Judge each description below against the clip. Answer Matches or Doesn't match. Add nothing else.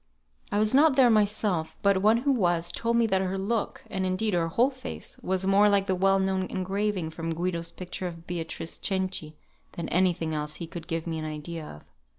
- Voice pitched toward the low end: Doesn't match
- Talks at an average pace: Doesn't match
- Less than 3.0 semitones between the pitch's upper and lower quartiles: Doesn't match